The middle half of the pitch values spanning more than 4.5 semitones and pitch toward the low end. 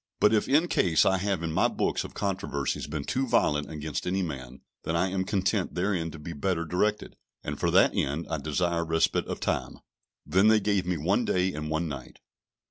No: average, 3.8 semitones; very low, 85 Hz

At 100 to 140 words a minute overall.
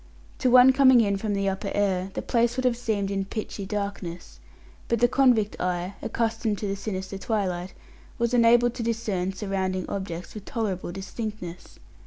No: average, 170 wpm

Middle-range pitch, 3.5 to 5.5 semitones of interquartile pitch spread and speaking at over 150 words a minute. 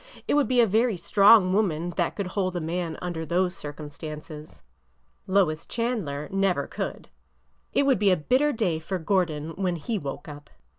Yes: medium, 180 Hz; average, 4.5 semitones; average, 170 wpm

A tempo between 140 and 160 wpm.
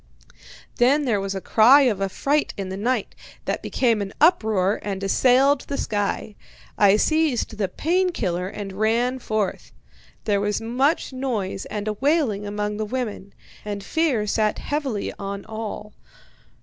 Yes: average, 150 wpm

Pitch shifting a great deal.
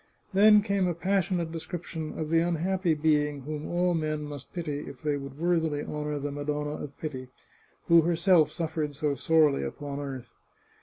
No: narrow, 2.6 semitones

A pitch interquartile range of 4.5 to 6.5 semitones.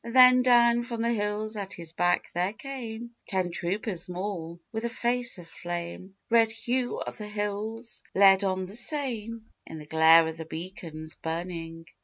Yes: average, 5.2 semitones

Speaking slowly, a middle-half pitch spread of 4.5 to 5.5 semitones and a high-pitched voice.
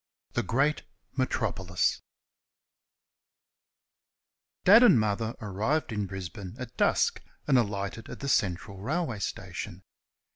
No: slow, 105 wpm; average, 5.0 semitones; low, 110 Hz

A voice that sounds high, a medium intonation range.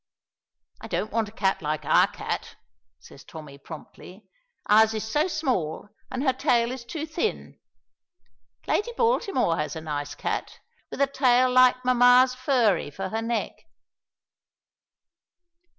No: high, 235 Hz; wide, 7.5 semitones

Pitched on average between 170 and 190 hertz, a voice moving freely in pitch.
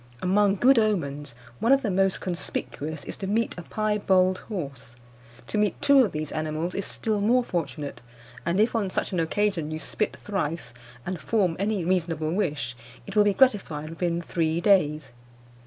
No: medium, 185 Hz; average, 4.9 semitones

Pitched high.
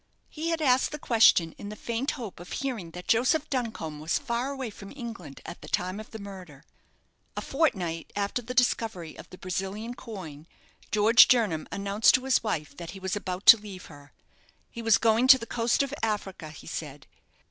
Yes: high, 210 Hz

